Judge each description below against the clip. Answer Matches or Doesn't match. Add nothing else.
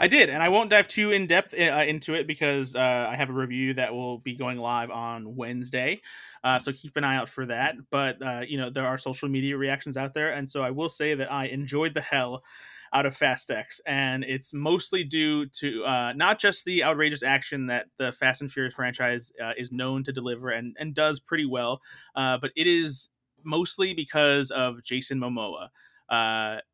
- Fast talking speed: Matches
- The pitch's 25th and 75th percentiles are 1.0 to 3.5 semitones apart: Matches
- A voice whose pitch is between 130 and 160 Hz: Matches